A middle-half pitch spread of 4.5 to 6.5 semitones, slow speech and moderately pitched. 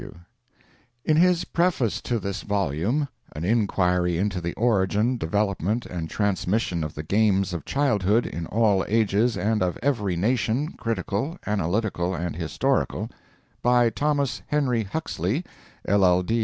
No: average, 5.1 semitones; slow, 130 wpm; low, 105 Hz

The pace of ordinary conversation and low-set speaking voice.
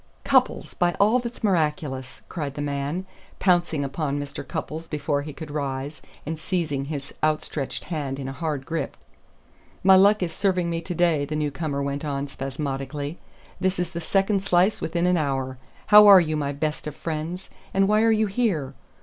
No: average, 180 wpm; medium, 155 Hz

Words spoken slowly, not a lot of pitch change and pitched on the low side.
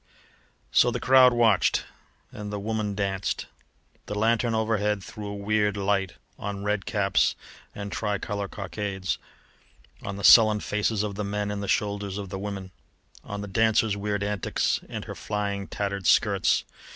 No: average, 155 wpm; narrow, 1.0 semitones; low, 105 Hz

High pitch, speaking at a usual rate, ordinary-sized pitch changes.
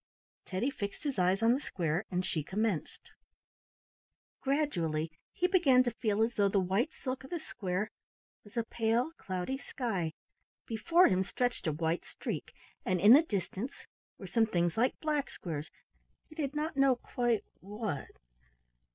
No: high, 220 Hz; average, 160 wpm; wide, 6.3 semitones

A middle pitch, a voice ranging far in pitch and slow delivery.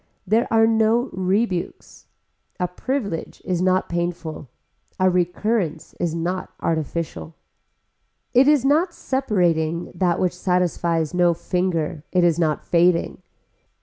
No: medium, 180 Hz; average, 4.1 semitones; slow, 115 wpm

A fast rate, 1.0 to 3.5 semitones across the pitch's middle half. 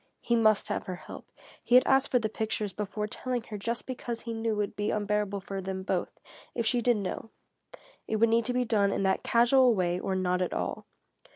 Yes: fast, 225 wpm; average, 3.1 semitones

